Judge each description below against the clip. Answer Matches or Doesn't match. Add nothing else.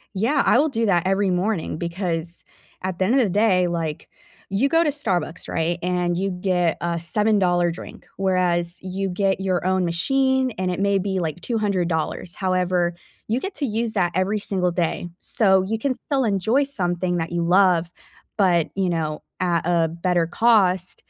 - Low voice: Doesn't match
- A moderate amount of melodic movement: Matches